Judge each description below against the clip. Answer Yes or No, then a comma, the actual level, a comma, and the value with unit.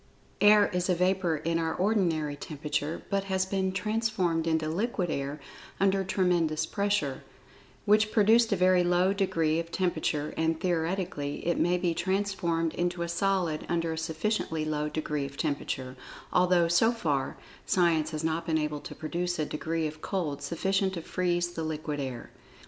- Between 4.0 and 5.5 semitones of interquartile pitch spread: No, average, 3.3 semitones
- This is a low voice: No, medium, 170 Hz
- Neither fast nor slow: Yes, average, 165 wpm